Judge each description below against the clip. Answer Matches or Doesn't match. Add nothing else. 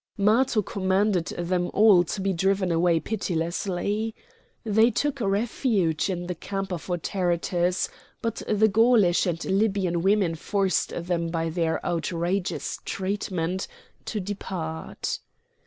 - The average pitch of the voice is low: Doesn't match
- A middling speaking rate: Doesn't match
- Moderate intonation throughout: Matches